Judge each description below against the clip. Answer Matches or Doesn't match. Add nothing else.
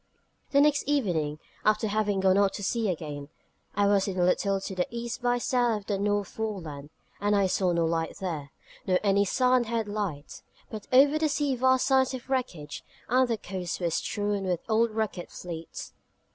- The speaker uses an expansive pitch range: Doesn't match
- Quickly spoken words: Doesn't match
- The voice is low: Doesn't match